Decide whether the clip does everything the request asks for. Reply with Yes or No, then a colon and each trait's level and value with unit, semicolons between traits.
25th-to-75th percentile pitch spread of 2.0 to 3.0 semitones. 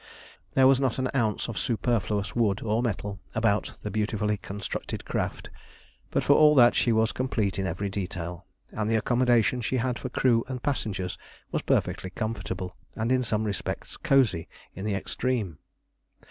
No: average, 3.8 semitones